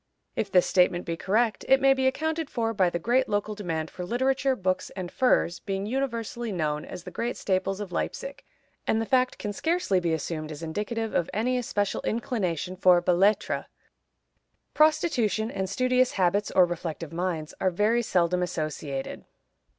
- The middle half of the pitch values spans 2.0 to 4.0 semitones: No, average, 5.3 semitones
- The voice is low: No, high, 200 Hz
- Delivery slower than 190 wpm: Yes, average, 170 wpm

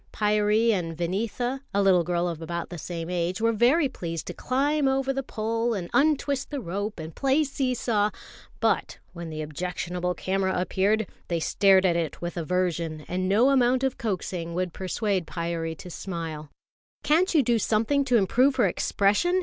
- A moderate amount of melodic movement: No, wide, 6.1 semitones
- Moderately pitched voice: No, high, 195 Hz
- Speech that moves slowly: No, average, 175 wpm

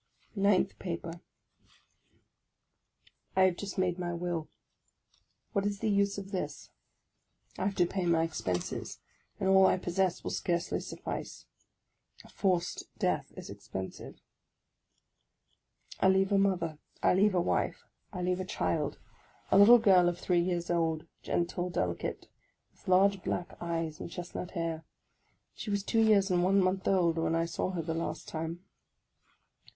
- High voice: No, medium, 180 Hz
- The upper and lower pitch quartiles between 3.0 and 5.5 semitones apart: No, narrow, 2.4 semitones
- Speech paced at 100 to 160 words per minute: Yes, average, 155 wpm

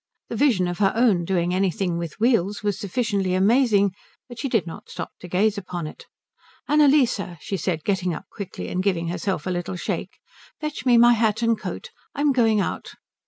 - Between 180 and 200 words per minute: Yes, average, 190 wpm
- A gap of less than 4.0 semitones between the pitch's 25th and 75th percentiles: No, average, 4.7 semitones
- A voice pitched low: No, high, 200 Hz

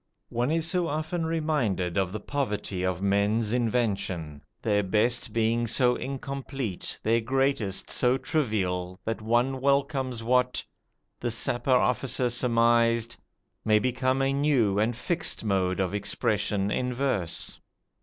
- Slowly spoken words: Yes, slow, 130 wpm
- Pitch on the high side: No, low, 120 Hz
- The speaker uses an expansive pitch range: No, average, 4.3 semitones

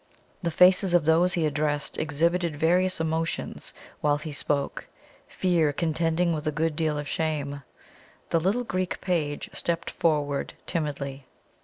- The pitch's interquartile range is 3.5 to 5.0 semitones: No, average, 2.7 semitones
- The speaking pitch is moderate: Yes, medium, 160 Hz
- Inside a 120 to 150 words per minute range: Yes, average, 140 wpm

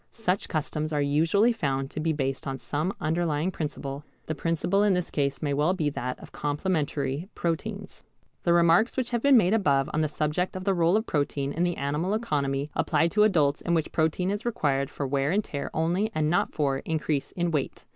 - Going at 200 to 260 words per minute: Yes, fast, 205 wpm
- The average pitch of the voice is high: No, medium, 155 Hz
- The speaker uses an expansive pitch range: No, average, 4.0 semitones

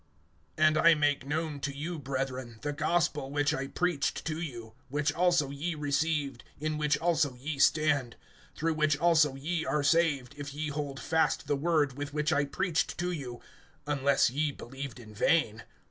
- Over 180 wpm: No, average, 175 wpm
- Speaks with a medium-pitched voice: Yes, medium, 145 Hz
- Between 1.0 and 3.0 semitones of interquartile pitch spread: Yes, narrow, 2.4 semitones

